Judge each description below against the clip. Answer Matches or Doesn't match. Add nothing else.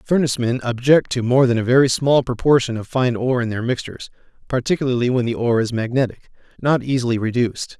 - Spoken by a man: Matches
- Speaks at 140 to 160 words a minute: Doesn't match